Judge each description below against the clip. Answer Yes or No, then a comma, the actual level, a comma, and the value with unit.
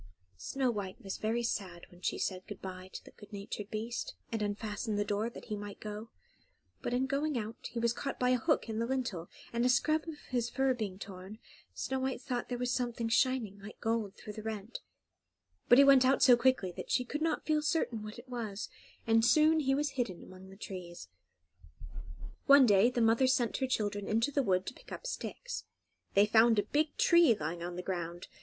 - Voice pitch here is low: No, high, 230 Hz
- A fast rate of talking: Yes, fast, 215 wpm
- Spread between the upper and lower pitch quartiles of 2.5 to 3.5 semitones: No, average, 4.2 semitones